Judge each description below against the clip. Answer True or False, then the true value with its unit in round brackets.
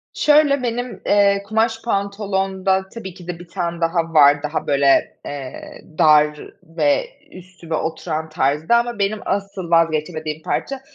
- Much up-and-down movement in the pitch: False (4.2 semitones)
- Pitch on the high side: False (180 Hz)